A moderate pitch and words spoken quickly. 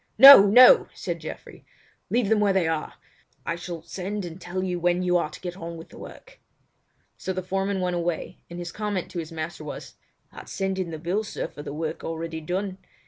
Yes: medium, 180 Hz; fast, 215 wpm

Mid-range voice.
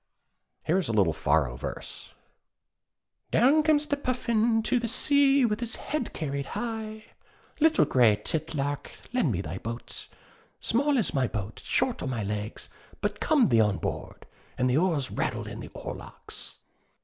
Yes: medium, 175 Hz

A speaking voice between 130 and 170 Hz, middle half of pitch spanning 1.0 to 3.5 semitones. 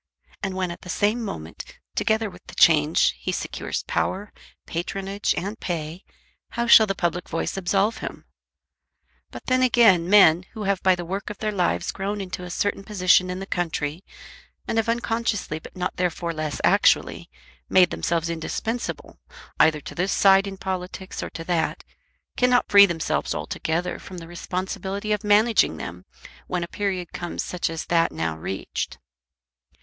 No: medium, 185 Hz; average, 3.2 semitones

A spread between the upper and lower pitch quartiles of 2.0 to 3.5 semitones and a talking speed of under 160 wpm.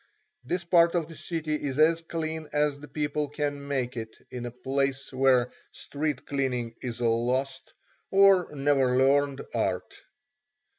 Yes: average, 3.1 semitones; average, 150 wpm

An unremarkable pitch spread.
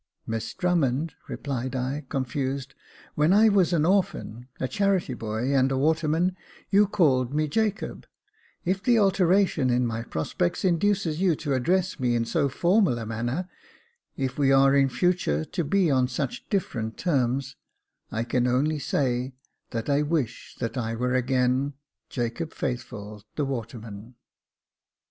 No: wide, 5.9 semitones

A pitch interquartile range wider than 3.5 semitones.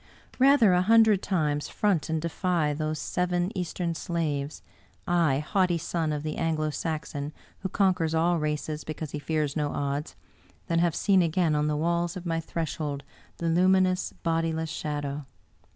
No: average, 2.9 semitones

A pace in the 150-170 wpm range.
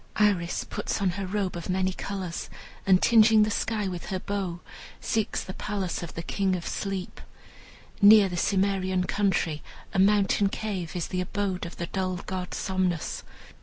Yes: average, 165 wpm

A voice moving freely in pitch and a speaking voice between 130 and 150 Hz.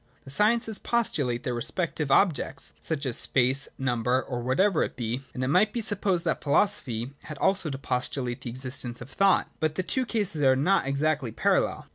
Yes: wide, 6.9 semitones; medium, 140 Hz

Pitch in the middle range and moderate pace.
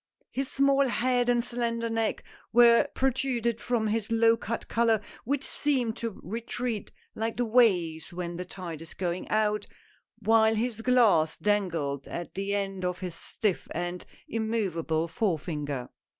No: high, 220 Hz; average, 150 wpm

